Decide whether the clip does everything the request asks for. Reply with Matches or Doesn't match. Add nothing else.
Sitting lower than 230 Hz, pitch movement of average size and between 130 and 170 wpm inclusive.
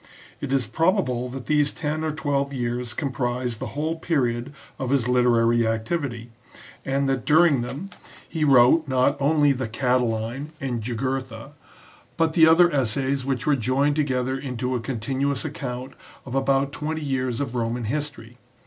Matches